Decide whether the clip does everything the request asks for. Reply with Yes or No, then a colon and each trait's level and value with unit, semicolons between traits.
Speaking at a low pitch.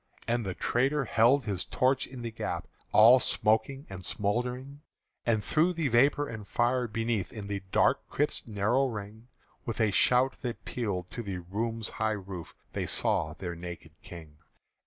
Yes: low, 115 Hz